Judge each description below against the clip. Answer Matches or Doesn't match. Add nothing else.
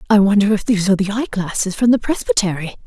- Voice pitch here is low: Doesn't match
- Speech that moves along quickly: Matches